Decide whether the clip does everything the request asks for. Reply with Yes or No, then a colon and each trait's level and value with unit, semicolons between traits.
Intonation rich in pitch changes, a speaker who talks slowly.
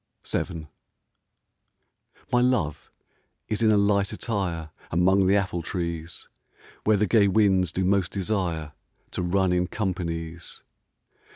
No: average, 3.0 semitones; slow, 120 wpm